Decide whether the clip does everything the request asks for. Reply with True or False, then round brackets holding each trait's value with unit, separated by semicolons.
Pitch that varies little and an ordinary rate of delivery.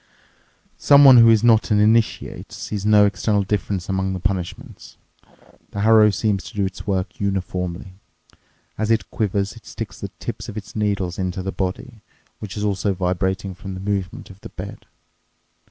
True (2.1 semitones; 170 wpm)